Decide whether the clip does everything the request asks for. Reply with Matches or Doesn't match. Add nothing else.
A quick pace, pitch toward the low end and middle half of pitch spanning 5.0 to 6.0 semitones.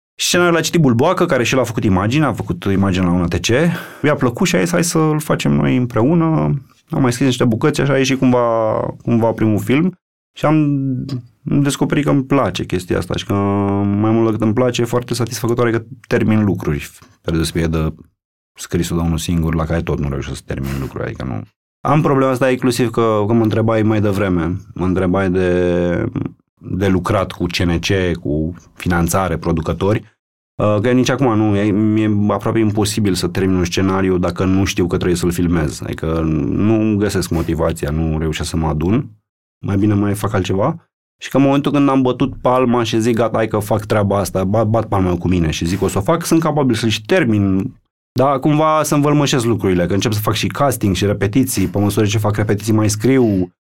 Matches